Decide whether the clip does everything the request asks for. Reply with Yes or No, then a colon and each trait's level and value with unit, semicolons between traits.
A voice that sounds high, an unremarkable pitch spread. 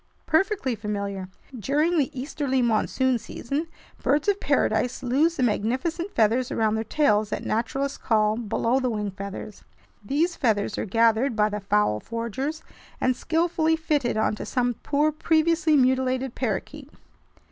No: very high, 255 Hz; wide, 5.7 semitones